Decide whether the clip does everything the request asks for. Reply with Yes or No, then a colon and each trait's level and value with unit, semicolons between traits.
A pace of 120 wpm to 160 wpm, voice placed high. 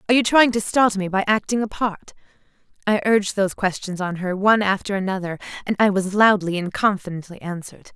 No: average, 195 wpm; high, 200 Hz